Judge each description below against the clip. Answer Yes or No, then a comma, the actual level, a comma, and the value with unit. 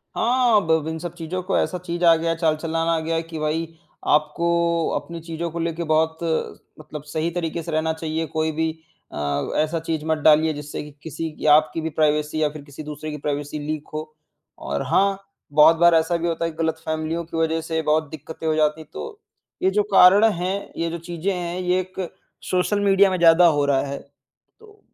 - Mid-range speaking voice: Yes, medium, 160 Hz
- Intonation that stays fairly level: Yes, narrow, 1.7 semitones